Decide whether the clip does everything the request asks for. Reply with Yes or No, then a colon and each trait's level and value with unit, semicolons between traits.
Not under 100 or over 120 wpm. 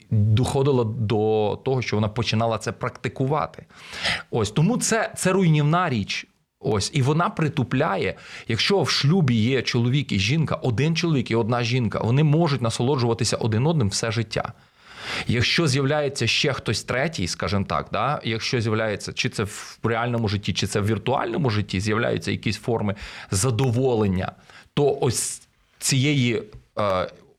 No: average, 140 wpm